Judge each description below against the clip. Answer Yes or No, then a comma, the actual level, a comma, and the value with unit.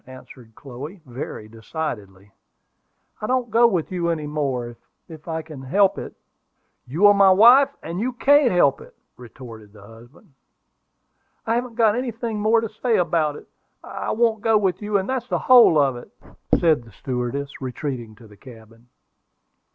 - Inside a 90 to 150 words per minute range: No, average, 165 wpm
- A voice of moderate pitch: Yes, medium, 160 Hz